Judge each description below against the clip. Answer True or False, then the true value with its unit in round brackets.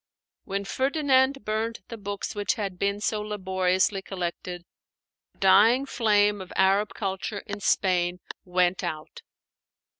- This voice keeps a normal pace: False (125 wpm)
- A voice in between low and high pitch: False (200 Hz)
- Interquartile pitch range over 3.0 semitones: False (2.4 semitones)